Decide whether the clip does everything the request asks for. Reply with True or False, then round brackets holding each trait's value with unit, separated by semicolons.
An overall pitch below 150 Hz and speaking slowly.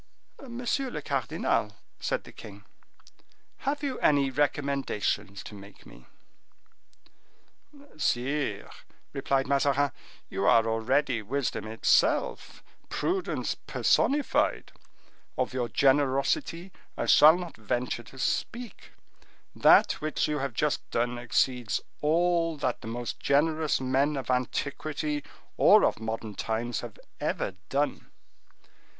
True (135 Hz; 110 wpm)